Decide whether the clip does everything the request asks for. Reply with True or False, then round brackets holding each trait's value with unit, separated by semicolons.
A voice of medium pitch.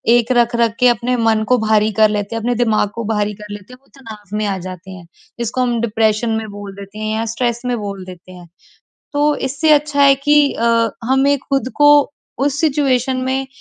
False (230 Hz)